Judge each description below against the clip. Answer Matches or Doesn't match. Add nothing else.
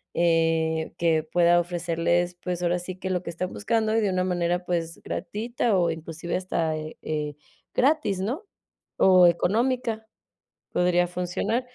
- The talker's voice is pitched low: Doesn't match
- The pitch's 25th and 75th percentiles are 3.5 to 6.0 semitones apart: Doesn't match